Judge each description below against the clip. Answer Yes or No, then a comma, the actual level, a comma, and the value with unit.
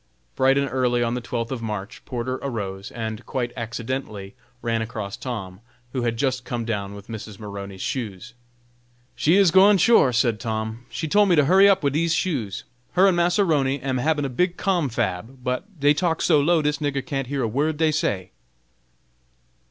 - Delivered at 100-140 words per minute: No, average, 190 wpm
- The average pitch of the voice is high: No, low, 130 Hz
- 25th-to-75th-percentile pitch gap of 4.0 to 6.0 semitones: Yes, wide, 5.5 semitones